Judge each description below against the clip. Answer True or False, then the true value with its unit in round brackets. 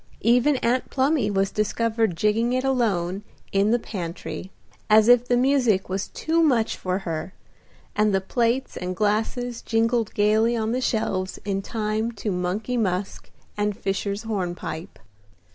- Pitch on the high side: True (215 Hz)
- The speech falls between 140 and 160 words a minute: True (145 wpm)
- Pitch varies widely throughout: False (3.7 semitones)